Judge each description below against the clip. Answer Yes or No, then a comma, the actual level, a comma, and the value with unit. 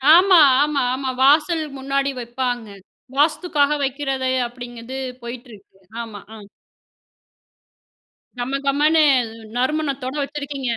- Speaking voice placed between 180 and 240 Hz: No, very high, 275 Hz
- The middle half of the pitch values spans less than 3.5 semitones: Yes, average, 3.0 semitones